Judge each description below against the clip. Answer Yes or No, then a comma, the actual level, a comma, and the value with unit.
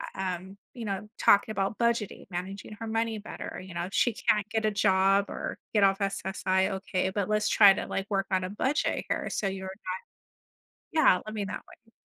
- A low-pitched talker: No, high, 195 Hz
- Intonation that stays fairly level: Yes, narrow, 2.1 semitones